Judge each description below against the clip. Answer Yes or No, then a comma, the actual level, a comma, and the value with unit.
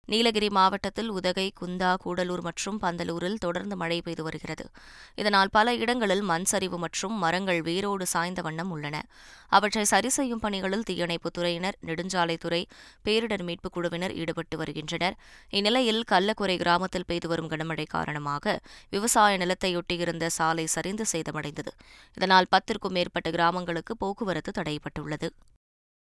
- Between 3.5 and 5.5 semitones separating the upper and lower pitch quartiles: No, average, 3.0 semitones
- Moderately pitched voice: Yes, medium, 180 Hz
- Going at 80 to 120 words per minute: Yes, average, 115 wpm